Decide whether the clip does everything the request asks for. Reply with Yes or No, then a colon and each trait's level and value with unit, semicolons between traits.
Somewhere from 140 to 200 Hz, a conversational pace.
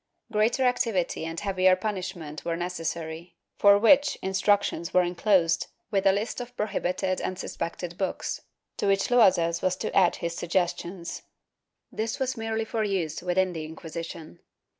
Yes: medium, 185 Hz; average, 145 wpm